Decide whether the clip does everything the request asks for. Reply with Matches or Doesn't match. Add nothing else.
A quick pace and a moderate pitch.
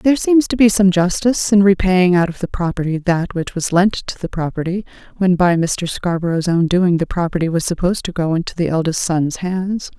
Matches